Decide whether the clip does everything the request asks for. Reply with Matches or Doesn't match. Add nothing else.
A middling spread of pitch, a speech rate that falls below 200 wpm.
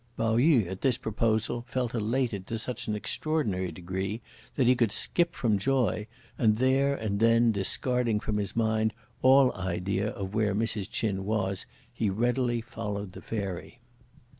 Matches